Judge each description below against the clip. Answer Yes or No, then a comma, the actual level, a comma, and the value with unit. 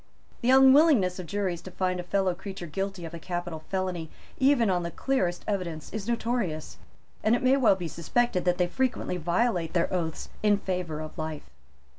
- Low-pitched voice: No, medium, 185 Hz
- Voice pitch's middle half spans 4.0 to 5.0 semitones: Yes, average, 4.4 semitones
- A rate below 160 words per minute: No, average, 185 wpm